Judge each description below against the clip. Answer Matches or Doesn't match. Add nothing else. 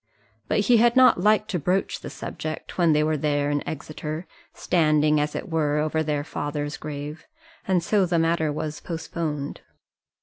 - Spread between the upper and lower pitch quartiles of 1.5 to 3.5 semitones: Matches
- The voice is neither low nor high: Matches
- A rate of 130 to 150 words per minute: Doesn't match